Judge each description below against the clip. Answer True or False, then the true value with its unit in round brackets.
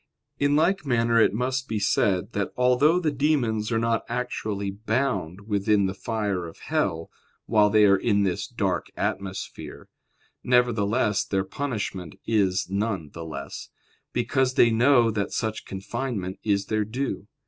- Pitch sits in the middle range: False (110 Hz)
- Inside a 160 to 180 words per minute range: False (150 wpm)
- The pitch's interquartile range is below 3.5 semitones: False (4.0 semitones)